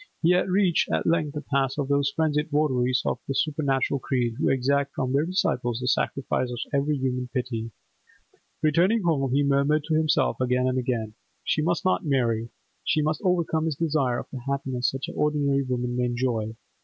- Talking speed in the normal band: Yes, average, 190 wpm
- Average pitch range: Yes, average, 3.4 semitones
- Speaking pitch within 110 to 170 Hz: Yes, medium, 140 Hz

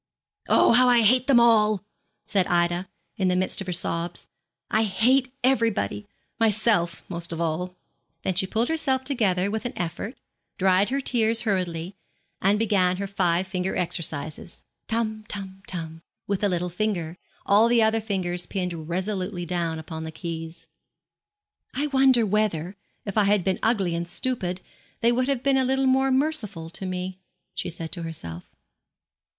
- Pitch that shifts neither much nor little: Yes, average, 4.6 semitones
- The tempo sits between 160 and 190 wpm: Yes, average, 165 wpm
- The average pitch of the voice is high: Yes, high, 195 Hz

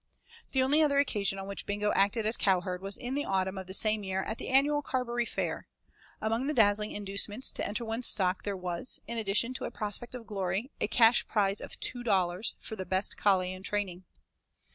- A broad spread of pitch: No, average, 3.8 semitones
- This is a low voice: No, high, 205 Hz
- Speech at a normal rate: No, fast, 210 wpm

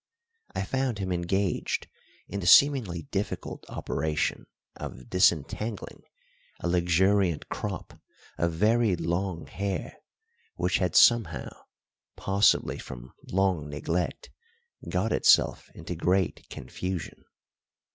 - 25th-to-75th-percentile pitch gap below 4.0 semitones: Yes, average, 2.9 semitones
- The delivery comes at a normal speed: No, slow, 100 wpm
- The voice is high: No, very low, 90 Hz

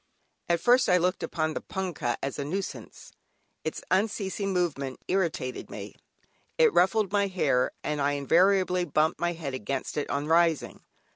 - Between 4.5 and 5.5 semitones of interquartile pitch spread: Yes, average, 4.9 semitones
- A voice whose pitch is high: No, medium, 170 Hz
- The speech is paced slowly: No, average, 155 wpm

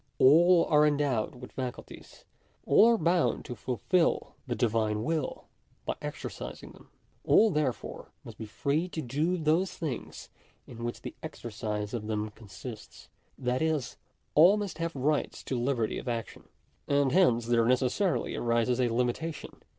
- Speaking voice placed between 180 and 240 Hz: No, low, 130 Hz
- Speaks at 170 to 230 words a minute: No, average, 145 wpm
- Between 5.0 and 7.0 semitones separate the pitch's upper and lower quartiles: Yes, average, 5.3 semitones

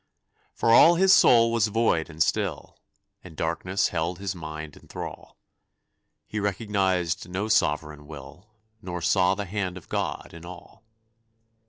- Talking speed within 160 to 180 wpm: No, average, 145 wpm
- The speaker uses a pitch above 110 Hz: No, very low, 90 Hz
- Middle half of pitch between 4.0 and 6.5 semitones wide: Yes, average, 4.3 semitones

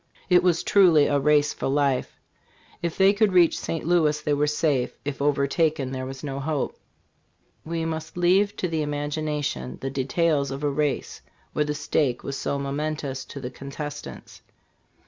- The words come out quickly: No, average, 165 wpm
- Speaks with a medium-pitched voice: Yes, medium, 150 Hz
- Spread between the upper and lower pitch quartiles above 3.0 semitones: No, average, 2.7 semitones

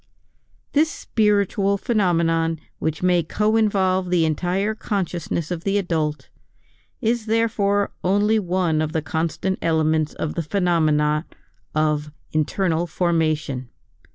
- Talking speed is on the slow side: Yes, slow, 115 wpm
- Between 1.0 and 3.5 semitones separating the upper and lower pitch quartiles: No, average, 4.1 semitones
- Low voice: No, medium, 175 Hz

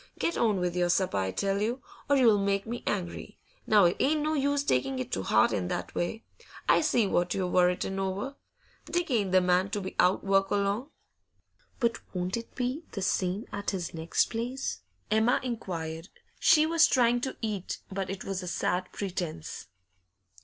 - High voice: Yes, high, 200 Hz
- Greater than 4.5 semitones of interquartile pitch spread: Yes, average, 4.9 semitones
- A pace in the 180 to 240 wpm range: Yes, average, 190 wpm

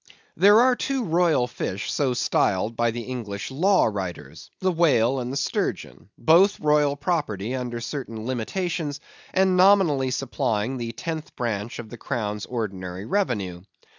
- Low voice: Yes, low, 130 Hz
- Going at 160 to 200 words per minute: No, average, 140 wpm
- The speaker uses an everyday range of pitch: No, wide, 6.8 semitones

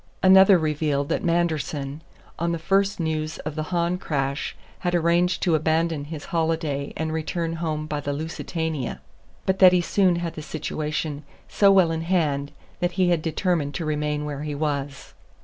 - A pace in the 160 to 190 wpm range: Yes, average, 170 wpm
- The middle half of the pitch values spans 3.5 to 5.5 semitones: No, narrow, 2.5 semitones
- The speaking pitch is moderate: Yes, medium, 160 Hz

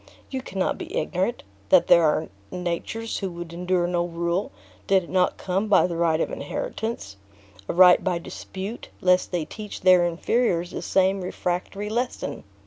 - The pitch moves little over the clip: Yes, narrow, 2.3 semitones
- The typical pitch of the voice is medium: Yes, medium, 180 Hz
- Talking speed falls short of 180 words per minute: Yes, average, 165 wpm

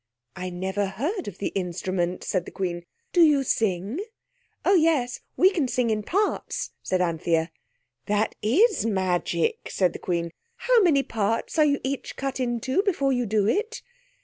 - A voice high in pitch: Yes, high, 225 Hz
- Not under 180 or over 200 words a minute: No, average, 165 wpm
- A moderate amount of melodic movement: No, wide, 7.9 semitones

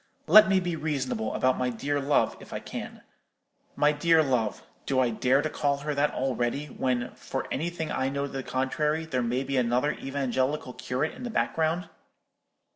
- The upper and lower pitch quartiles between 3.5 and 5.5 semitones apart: No, average, 3.0 semitones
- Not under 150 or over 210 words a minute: Yes, average, 180 wpm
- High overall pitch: No, medium, 140 Hz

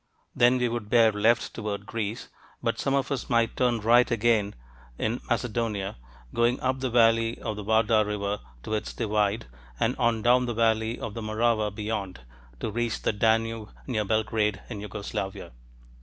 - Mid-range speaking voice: No, low, 110 Hz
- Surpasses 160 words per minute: Yes, average, 170 wpm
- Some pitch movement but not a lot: No, narrow, 2.0 semitones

